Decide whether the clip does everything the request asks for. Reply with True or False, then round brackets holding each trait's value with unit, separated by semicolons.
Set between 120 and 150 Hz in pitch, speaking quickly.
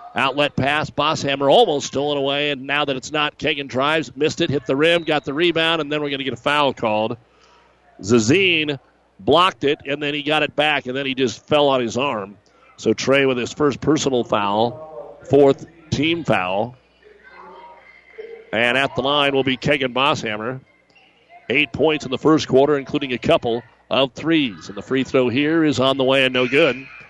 False (140 Hz; 195 wpm)